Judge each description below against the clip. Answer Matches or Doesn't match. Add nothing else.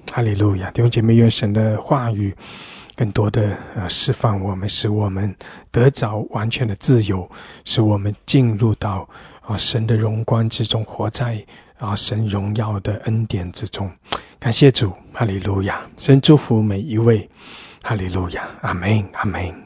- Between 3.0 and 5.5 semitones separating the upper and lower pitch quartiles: Doesn't match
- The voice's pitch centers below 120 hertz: Matches